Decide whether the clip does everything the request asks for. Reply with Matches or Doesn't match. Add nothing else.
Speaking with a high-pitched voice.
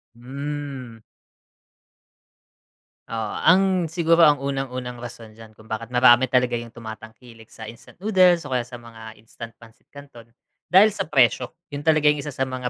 Doesn't match